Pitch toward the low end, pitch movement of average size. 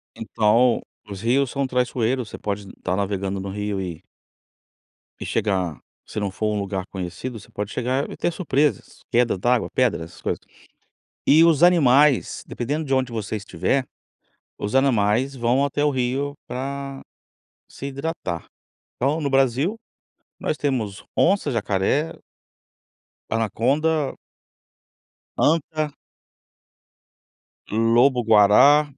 Yes: low, 125 Hz; average, 5.0 semitones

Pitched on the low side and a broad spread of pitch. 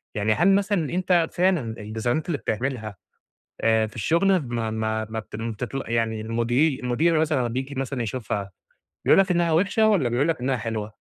Yes: low, 125 Hz; wide, 6.7 semitones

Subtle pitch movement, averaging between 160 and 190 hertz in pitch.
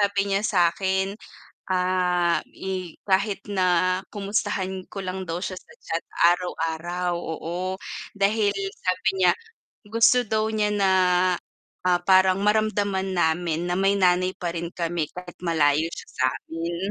Yes: narrow, 2.2 semitones; medium, 185 Hz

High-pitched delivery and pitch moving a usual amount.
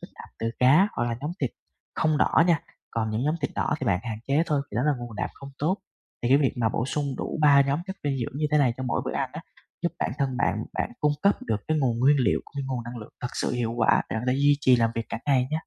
No: low, 130 Hz; average, 3.8 semitones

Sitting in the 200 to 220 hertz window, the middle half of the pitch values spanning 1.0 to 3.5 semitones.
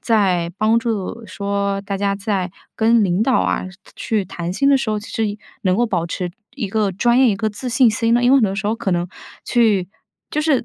Yes: high, 210 Hz; average, 3.2 semitones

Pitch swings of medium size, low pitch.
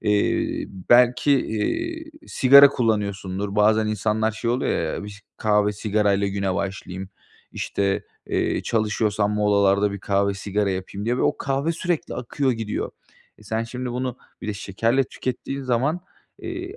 Yes: average, 3.9 semitones; low, 110 Hz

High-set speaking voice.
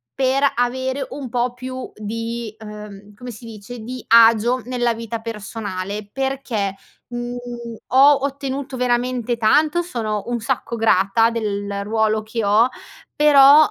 Yes: high, 235 Hz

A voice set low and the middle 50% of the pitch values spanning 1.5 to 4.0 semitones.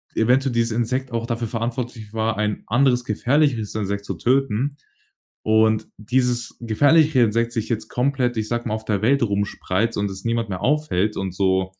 Yes: low, 115 Hz; average, 2.7 semitones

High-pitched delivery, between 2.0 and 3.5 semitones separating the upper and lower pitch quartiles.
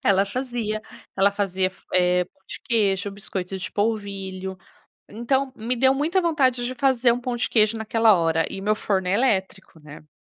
No: high, 210 Hz; average, 4.2 semitones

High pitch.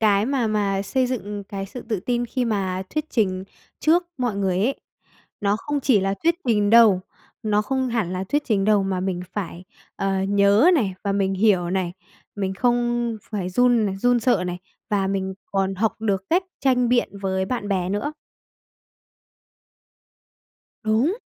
Yes: high, 205 Hz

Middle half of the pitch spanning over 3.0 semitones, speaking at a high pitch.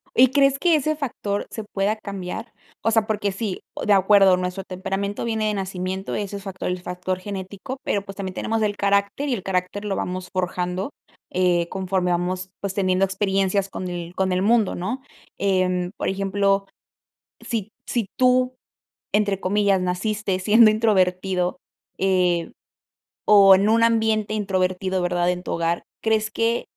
No: narrow, 2.5 semitones; high, 195 Hz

